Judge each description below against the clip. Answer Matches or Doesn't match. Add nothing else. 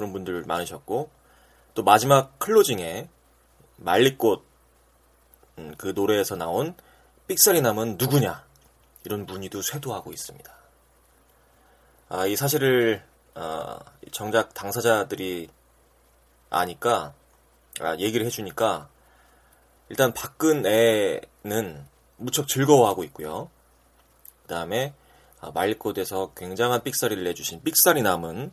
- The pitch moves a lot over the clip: Matches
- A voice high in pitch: Doesn't match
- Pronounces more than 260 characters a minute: Doesn't match